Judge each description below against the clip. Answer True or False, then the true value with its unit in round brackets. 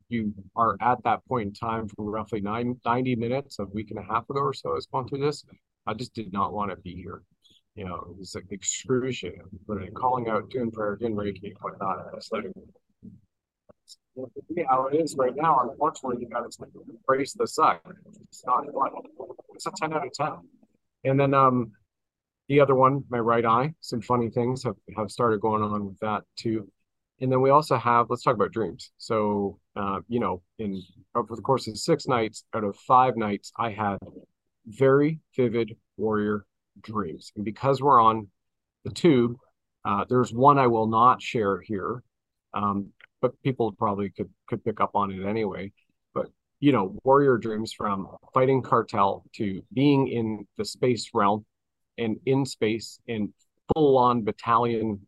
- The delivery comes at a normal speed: True (180 wpm)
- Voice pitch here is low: True (115 Hz)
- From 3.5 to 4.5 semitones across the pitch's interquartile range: True (3.8 semitones)